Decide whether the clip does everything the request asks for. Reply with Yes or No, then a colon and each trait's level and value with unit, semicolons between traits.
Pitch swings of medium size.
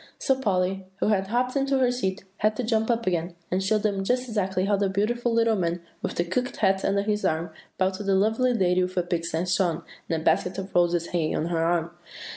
Yes: average, 3.8 semitones